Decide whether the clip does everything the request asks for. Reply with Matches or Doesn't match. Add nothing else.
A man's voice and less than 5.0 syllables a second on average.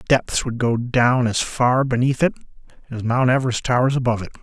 Doesn't match